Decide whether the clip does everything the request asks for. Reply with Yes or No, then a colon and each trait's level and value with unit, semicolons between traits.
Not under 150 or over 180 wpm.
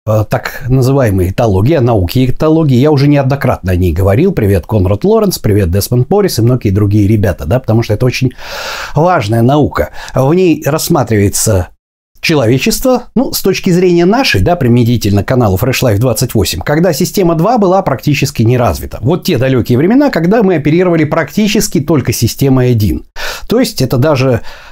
Yes: fast, 160 wpm